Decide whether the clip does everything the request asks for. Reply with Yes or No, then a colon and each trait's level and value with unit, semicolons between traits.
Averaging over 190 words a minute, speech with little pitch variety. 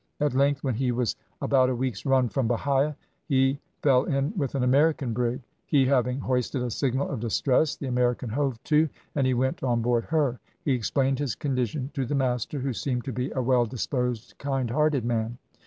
Yes: average, 200 wpm; narrow, 2.1 semitones